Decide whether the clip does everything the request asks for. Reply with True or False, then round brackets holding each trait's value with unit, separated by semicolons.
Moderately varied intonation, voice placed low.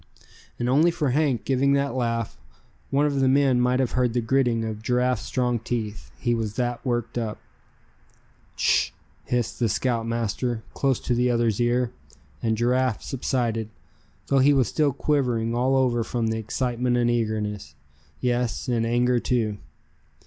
False (2.0 semitones; 120 Hz)